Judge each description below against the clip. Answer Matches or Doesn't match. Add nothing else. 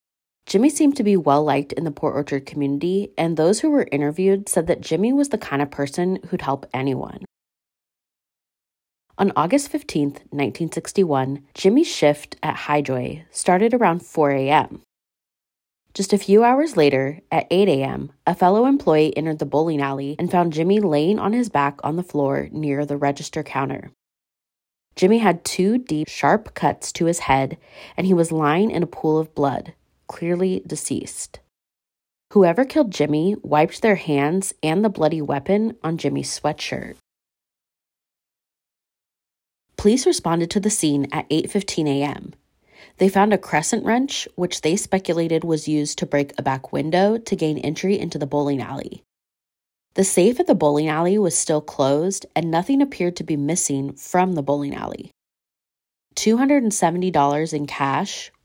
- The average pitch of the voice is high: Doesn't match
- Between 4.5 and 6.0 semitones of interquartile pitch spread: Matches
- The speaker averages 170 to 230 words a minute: Doesn't match